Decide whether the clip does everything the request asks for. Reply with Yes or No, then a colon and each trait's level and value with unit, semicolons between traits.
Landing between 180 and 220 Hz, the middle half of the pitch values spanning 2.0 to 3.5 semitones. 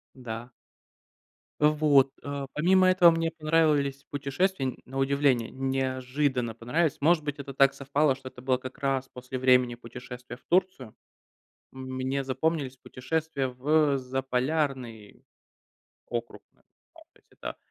No: low, 135 Hz; average, 2.8 semitones